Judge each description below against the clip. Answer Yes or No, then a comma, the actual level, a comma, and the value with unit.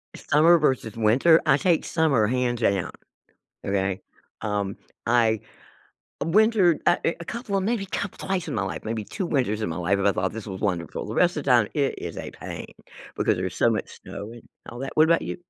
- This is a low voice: Yes, low, 120 Hz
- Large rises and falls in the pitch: Yes, wide, 8.5 semitones